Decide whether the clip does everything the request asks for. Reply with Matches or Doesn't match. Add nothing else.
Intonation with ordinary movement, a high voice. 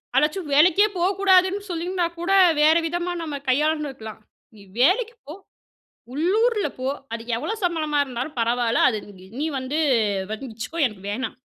Doesn't match